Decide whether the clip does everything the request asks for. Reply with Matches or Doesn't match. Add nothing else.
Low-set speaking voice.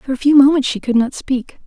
Doesn't match